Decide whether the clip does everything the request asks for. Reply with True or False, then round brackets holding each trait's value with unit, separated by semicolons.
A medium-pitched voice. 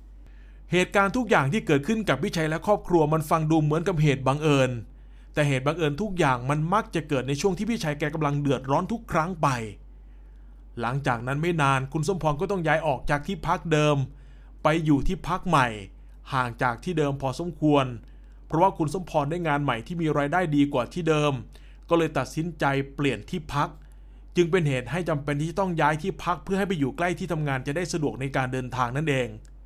True (150 Hz)